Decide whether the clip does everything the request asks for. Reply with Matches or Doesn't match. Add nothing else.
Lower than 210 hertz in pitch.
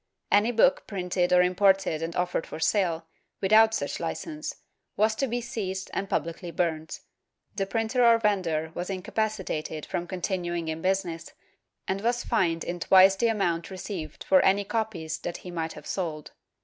Matches